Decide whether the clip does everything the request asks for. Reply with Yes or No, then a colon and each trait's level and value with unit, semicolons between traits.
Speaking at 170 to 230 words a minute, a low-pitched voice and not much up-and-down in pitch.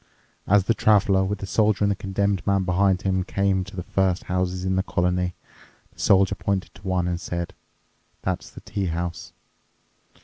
Yes: average, 180 wpm; very low, 95 Hz; narrow, 1.6 semitones